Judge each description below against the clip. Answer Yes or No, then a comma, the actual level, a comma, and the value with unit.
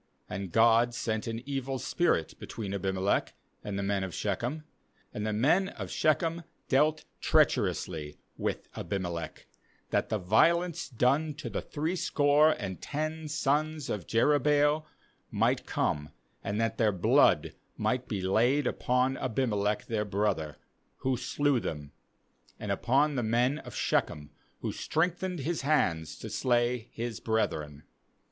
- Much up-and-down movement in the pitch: Yes, wide, 6.5 semitones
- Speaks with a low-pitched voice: Yes, low, 120 Hz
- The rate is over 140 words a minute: No, slow, 135 wpm